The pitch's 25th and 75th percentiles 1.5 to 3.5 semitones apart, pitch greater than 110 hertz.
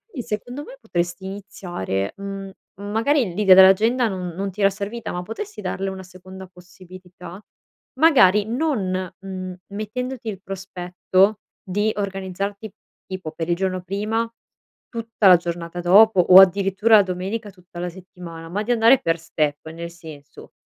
Yes: average, 2.9 semitones; high, 190 Hz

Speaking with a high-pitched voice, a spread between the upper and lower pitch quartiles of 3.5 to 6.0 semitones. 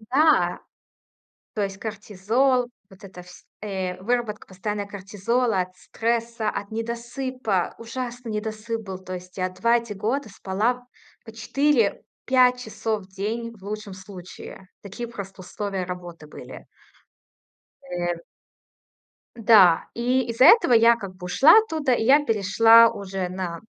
Yes: high, 215 Hz; average, 3.8 semitones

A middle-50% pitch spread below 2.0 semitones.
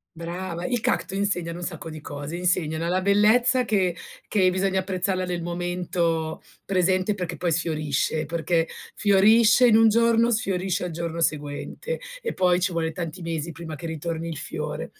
No: average, 2.9 semitones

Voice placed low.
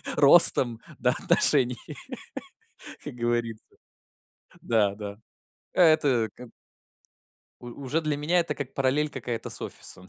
Yes: low, 125 Hz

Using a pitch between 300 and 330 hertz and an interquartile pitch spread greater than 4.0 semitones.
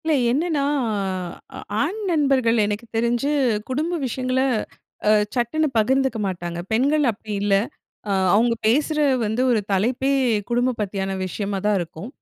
No: high, 240 Hz; average, 4.6 semitones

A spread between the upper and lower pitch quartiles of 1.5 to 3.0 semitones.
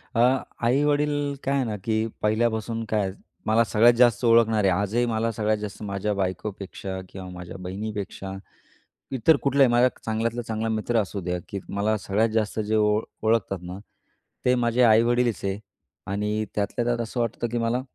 Yes: narrow, 2.6 semitones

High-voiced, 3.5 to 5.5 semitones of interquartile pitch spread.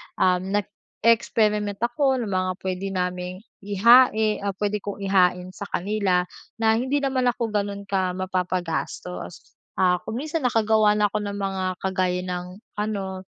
No: high, 200 Hz; average, 2.9 semitones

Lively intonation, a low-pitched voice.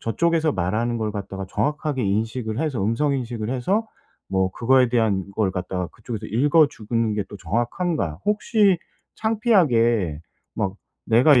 Yes: wide, 6.2 semitones; low, 115 Hz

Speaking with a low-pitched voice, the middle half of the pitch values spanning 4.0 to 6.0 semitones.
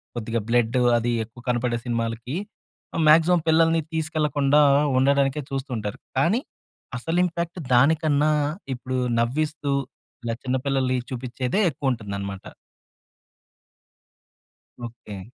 Yes: low, 130 Hz; average, 4.6 semitones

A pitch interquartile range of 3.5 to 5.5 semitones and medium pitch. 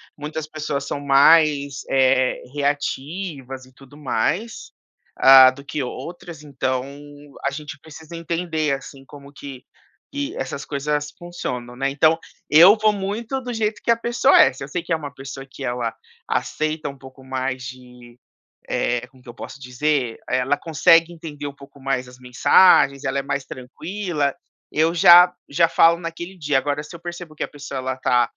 Yes: average, 3.9 semitones; medium, 145 Hz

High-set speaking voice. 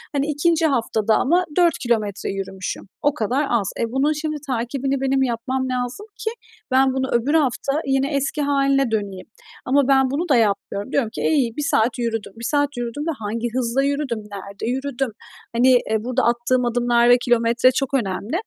Yes: very high, 255 Hz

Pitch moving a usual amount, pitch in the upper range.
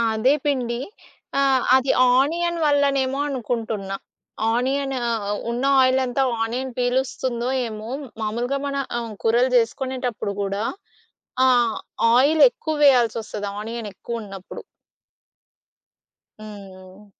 Yes: average, 3.4 semitones; high, 245 Hz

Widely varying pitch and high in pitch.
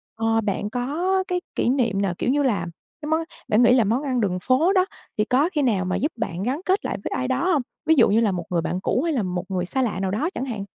Yes: wide, 6.5 semitones; high, 245 Hz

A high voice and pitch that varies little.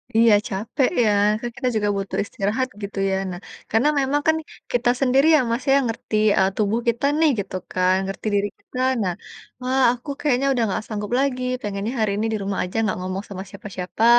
No: high, 220 Hz; average, 4.2 semitones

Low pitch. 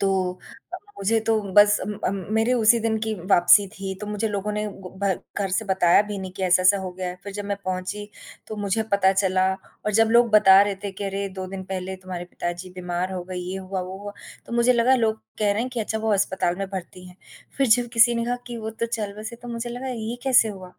No: high, 200 Hz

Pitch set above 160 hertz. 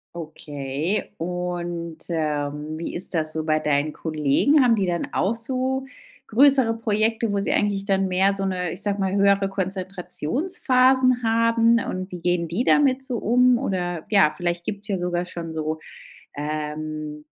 Yes: medium, 185 Hz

